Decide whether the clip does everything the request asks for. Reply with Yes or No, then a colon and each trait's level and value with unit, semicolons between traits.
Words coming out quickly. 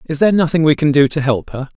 Yes: fast, 300 wpm